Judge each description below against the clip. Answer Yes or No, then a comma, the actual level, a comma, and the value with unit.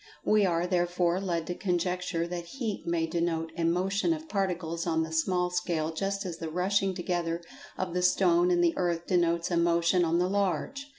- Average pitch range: No, narrow, 1.7 semitones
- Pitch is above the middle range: No, medium, 175 Hz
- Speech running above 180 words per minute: Yes, average, 190 wpm